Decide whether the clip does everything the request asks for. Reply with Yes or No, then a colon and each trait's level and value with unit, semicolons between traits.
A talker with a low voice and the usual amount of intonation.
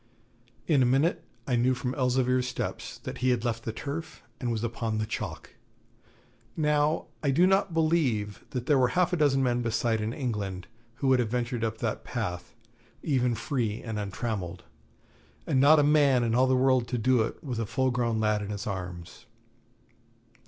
Yes: low, 125 Hz; average, 3.4 semitones